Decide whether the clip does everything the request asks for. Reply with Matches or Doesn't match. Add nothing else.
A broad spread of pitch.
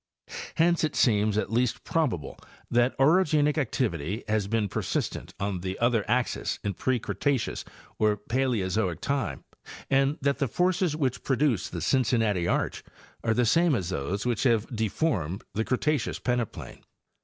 Doesn't match